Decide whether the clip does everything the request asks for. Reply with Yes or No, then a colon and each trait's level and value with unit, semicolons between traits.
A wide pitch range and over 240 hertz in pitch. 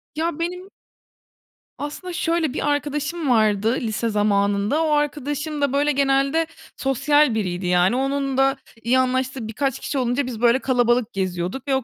No: average, 4.3 semitones; very high, 270 Hz